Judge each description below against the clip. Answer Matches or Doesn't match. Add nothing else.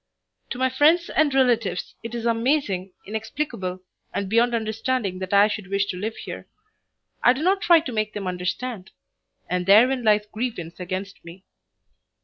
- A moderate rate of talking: Matches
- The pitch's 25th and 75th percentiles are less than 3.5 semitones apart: Doesn't match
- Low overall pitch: Doesn't match